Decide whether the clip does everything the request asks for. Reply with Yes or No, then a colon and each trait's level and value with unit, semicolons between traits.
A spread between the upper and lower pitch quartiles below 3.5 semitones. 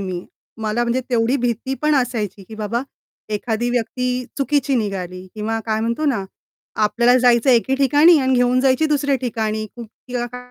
Yes: average, 3.1 semitones